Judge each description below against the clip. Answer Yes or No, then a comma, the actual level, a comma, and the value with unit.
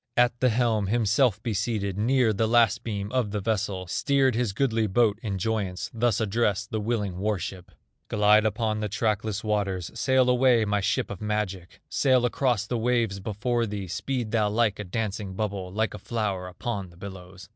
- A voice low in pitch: Yes, low, 105 Hz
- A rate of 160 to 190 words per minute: Yes, average, 185 wpm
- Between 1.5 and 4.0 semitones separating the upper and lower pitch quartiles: Yes, average, 2.9 semitones